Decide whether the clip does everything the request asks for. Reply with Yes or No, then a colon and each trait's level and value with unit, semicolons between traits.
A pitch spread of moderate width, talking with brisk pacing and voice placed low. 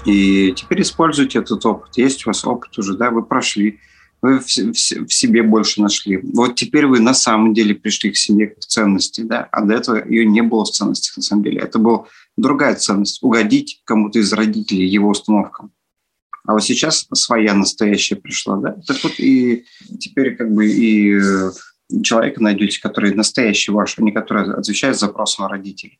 Yes: average, 3.3 semitones; fast, 175 wpm; low, 110 Hz